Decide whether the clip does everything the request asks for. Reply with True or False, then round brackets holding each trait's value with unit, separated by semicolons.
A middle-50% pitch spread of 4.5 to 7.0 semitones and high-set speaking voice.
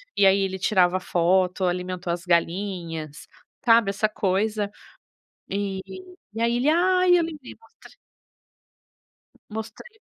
False (3.9 semitones; 195 Hz)